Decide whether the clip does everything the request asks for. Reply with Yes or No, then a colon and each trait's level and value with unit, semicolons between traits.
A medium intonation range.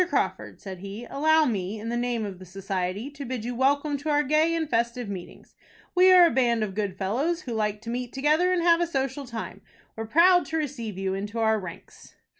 No: wide, 6.2 semitones